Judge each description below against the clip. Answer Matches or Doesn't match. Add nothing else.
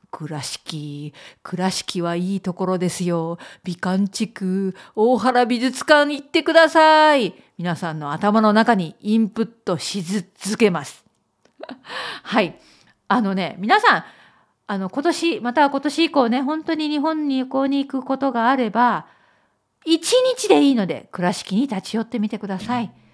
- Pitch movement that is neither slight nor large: Doesn't match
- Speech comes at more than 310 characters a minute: Doesn't match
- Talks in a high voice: Matches